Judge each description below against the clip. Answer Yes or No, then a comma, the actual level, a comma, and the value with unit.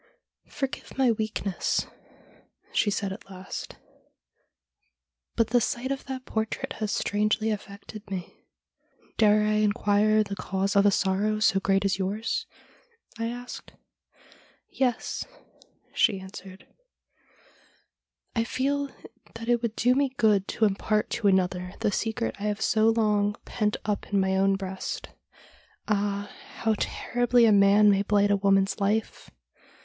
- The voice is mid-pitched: No, high, 210 Hz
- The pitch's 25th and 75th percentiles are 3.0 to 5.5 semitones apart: No, narrow, 2.5 semitones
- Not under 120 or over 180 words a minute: Yes, average, 150 wpm